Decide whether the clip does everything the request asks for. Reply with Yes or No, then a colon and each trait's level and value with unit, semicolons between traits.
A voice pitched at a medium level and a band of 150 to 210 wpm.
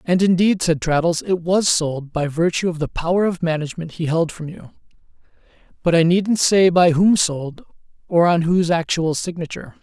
Yes: medium, 170 Hz; average, 185 wpm